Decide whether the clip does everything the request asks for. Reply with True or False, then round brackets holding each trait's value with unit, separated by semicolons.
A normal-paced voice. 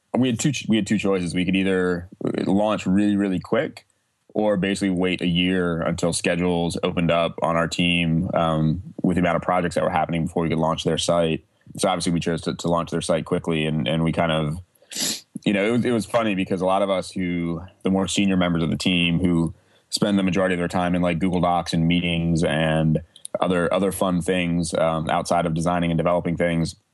False (225 wpm)